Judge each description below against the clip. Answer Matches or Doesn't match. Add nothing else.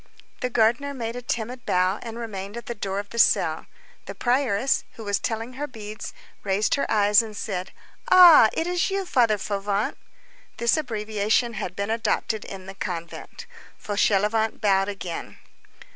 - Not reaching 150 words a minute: Doesn't match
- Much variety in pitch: Doesn't match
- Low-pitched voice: Doesn't match